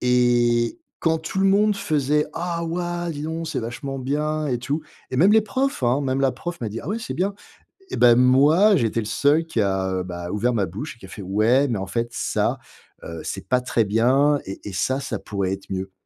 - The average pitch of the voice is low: Yes, low, 130 Hz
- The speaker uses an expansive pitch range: Yes, wide, 6.2 semitones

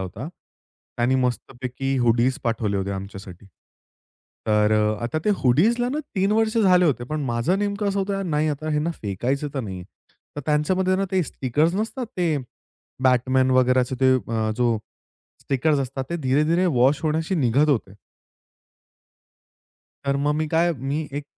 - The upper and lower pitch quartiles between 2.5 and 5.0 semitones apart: No, wide, 5.6 semitones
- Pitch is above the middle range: No, low, 135 Hz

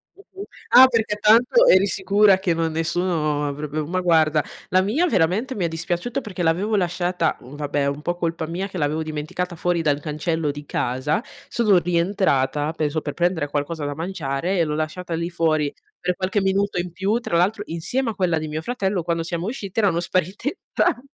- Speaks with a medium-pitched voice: Yes, medium, 175 Hz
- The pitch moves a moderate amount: Yes, average, 3.8 semitones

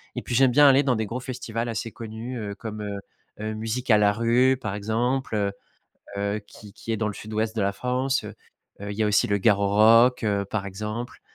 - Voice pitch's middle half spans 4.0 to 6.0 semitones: No, average, 2.8 semitones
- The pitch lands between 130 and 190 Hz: No, low, 110 Hz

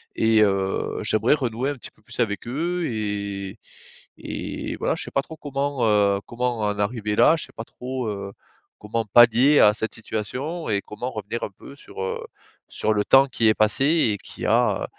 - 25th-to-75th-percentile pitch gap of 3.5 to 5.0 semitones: Yes, average, 3.8 semitones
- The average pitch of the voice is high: No, low, 110 Hz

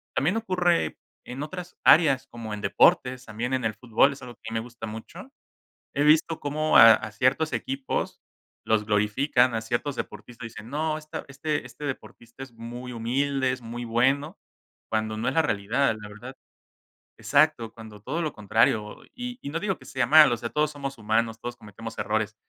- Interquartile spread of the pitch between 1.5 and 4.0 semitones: No, average, 4.5 semitones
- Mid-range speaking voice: No, low, 125 Hz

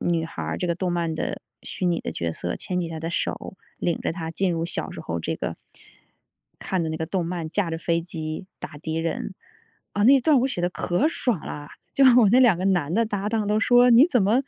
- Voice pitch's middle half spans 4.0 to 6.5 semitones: Yes, average, 4.6 semitones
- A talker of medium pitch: Yes, medium, 175 Hz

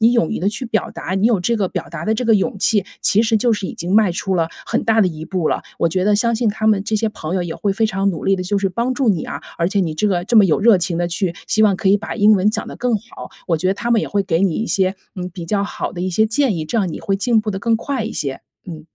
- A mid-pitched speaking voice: No, high, 200 Hz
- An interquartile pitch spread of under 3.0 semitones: No, average, 3.3 semitones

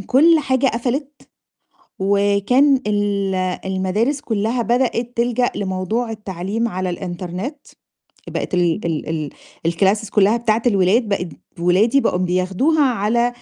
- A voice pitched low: No, high, 210 Hz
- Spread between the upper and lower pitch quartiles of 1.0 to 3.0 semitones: No, average, 4.5 semitones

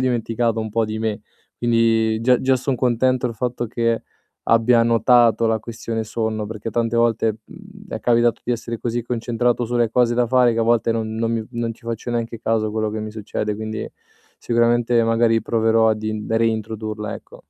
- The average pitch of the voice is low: Yes, low, 115 Hz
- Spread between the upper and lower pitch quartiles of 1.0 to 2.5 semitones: Yes, narrow, 1.3 semitones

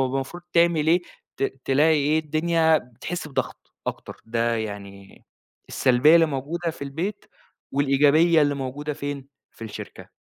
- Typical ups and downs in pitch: Yes, average, 3.4 semitones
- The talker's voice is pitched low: No, medium, 145 Hz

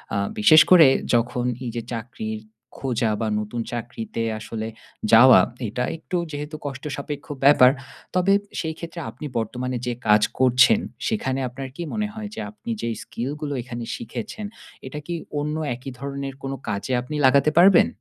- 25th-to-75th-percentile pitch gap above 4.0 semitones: Yes, average, 4.4 semitones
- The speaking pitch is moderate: No, low, 130 Hz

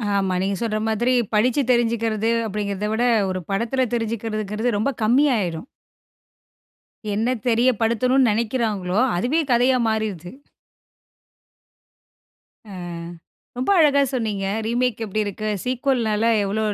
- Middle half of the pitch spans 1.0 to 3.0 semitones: Yes, average, 2.7 semitones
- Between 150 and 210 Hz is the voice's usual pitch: No, high, 225 Hz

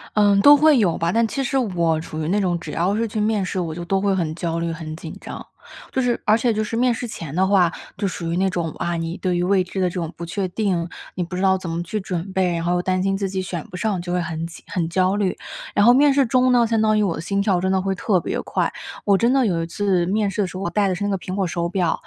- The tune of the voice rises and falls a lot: No, average, 3.4 semitones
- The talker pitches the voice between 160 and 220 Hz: Yes, high, 190 Hz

